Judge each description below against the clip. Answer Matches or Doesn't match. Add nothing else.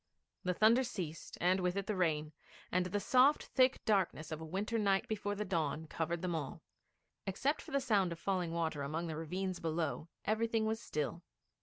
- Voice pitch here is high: Doesn't match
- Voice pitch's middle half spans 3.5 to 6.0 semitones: Matches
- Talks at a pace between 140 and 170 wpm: Doesn't match